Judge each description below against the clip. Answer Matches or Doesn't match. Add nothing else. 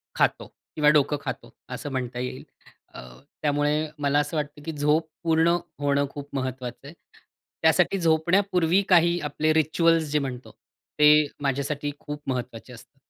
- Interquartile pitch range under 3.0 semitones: Matches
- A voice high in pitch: Doesn't match